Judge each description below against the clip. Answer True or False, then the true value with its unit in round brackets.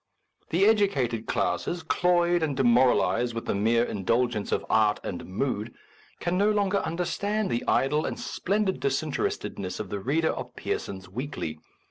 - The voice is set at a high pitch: False (135 Hz)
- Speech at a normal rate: True (150 wpm)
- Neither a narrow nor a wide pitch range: False (7.9 semitones)